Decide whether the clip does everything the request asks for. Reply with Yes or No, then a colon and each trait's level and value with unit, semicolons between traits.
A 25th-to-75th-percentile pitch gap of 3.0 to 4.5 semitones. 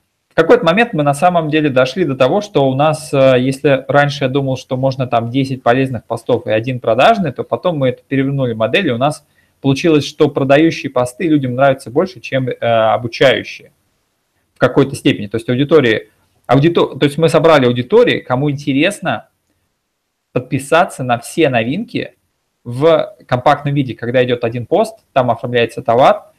Yes: average, 3.7 semitones